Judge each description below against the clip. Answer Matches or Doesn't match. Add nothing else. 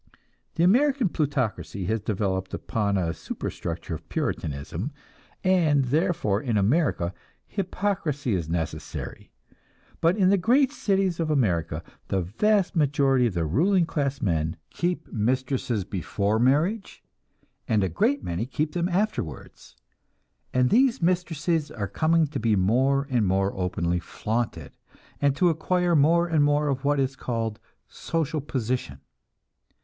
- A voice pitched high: Doesn't match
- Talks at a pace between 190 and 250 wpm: Doesn't match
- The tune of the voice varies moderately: Doesn't match